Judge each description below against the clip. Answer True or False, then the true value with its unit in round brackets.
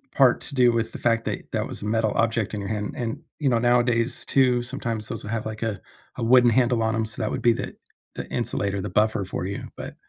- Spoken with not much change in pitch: True (2.0 semitones)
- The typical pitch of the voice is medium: False (115 Hz)